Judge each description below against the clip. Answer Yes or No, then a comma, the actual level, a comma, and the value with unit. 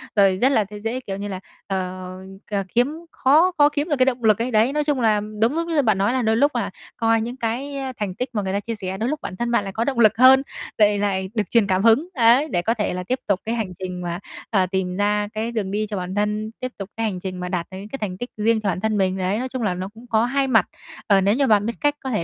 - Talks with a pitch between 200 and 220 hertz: Yes, high, 215 Hz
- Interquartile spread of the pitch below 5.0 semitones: Yes, average, 4.3 semitones